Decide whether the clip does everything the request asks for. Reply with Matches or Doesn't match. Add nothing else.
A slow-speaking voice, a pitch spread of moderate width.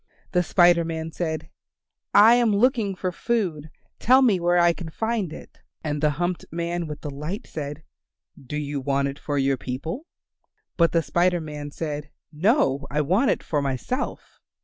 Doesn't match